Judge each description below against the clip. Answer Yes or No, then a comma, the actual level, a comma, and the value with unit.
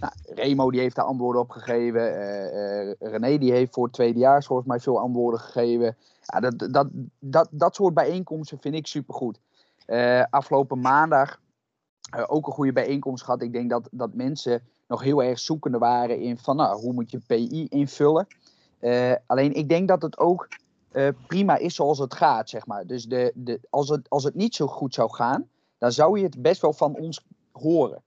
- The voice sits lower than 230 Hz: Yes, low, 135 Hz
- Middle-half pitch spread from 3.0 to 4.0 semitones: Yes, average, 3.5 semitones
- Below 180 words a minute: No, fast, 200 wpm